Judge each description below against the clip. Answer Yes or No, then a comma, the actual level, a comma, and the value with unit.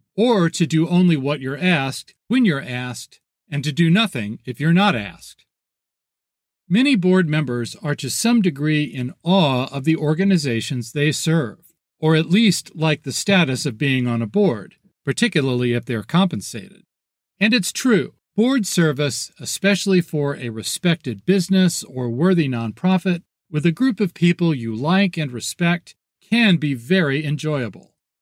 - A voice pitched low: No, medium, 160 Hz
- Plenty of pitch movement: Yes, wide, 6.0 semitones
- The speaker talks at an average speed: Yes, average, 155 wpm